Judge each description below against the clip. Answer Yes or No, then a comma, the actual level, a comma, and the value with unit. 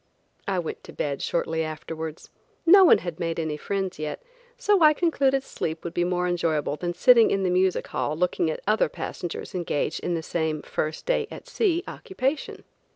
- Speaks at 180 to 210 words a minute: Yes, average, 185 wpm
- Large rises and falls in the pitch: Yes, wide, 7.8 semitones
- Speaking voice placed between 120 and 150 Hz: No, medium, 175 Hz